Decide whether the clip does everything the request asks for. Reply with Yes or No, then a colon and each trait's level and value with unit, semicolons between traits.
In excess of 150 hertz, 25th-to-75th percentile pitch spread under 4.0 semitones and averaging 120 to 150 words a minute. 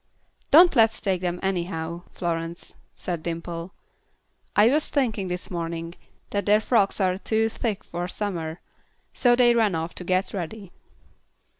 No: medium, 185 Hz; average, 4.3 semitones; average, 145 wpm